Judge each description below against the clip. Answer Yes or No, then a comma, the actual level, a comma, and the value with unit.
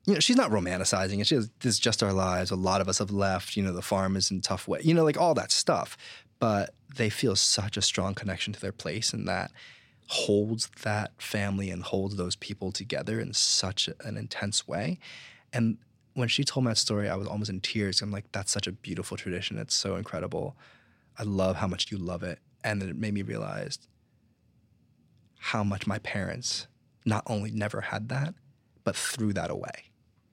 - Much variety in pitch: No, average, 3.3 semitones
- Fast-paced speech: Yes, fast, 210 wpm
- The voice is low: Yes, low, 105 Hz